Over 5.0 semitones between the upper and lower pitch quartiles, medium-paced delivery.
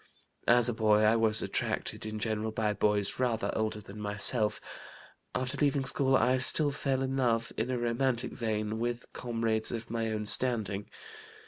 No: average, 2.7 semitones; average, 165 wpm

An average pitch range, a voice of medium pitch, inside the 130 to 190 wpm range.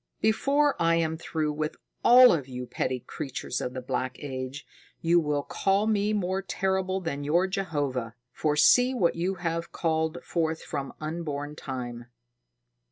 Yes: average, 5.0 semitones; medium, 160 Hz; average, 155 wpm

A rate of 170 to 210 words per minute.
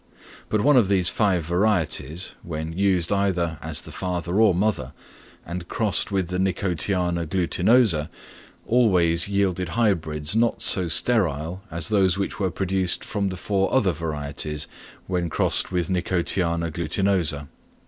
No: average, 140 wpm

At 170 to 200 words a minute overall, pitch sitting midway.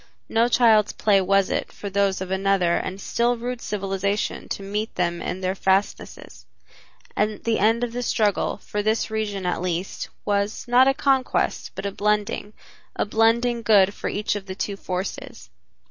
No: average, 175 wpm; high, 205 Hz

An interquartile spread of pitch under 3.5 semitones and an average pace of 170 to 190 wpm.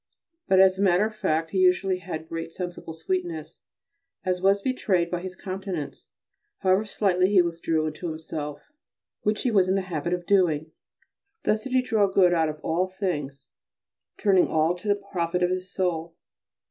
Yes: average, 2.8 semitones; average, 175 wpm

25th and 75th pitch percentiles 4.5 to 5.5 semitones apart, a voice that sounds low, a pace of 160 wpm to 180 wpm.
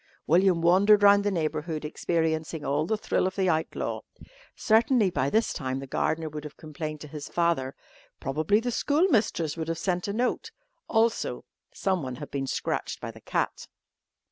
No: average, 4.9 semitones; medium, 165 Hz; average, 170 wpm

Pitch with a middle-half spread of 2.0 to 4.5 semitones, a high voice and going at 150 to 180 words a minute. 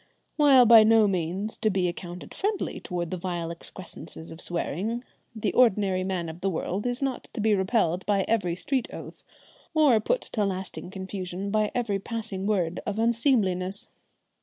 Yes: average, 3.9 semitones; high, 195 Hz; average, 165 wpm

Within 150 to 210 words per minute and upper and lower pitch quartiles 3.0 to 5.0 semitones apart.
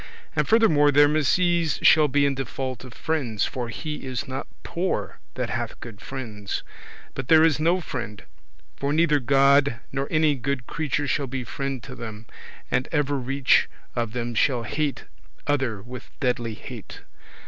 Yes: average, 160 wpm; average, 3.3 semitones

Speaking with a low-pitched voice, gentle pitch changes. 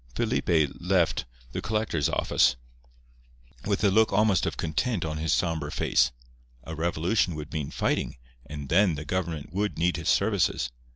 No: very low, 85 Hz; average, 4.1 semitones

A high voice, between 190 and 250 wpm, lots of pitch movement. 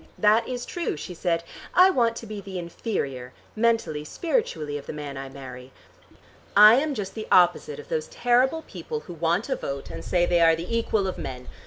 No: medium, 175 Hz; average, 200 wpm; wide, 7.5 semitones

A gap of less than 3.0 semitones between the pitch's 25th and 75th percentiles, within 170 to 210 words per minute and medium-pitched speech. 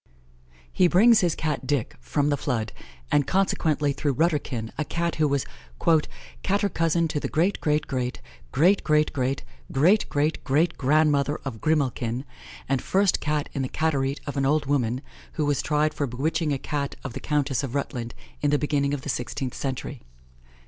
Yes: narrow, 2.6 semitones; average, 175 wpm; medium, 145 Hz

